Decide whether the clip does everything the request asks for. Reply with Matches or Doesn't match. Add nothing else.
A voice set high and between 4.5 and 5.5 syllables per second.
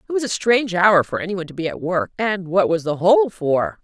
Doesn't match